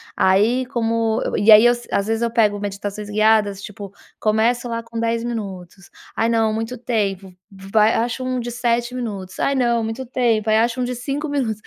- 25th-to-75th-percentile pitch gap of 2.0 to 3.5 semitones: Yes, narrow, 2.4 semitones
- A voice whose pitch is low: No, high, 225 Hz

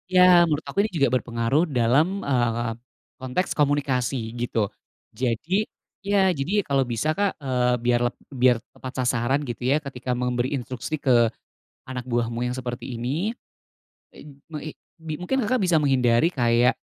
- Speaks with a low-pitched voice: Yes, low, 130 Hz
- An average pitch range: Yes, average, 3.6 semitones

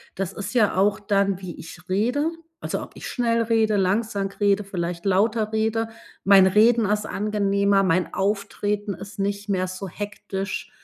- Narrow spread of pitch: Yes, narrow, 1.7 semitones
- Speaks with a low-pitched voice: No, high, 200 Hz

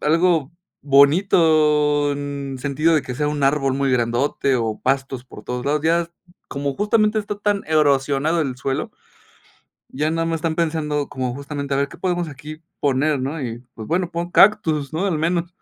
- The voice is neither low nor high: Yes, medium, 150 Hz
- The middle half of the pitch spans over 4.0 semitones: No, average, 3.3 semitones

